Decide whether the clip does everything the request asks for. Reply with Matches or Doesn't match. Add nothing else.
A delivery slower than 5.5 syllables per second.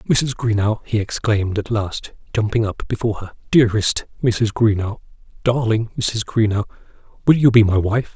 Matches